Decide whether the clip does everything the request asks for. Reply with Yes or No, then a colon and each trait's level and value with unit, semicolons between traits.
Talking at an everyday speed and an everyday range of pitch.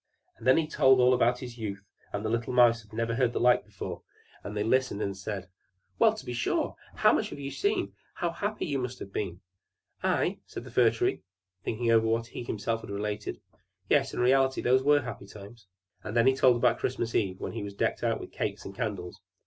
No: fast, 225 wpm; average, 3.6 semitones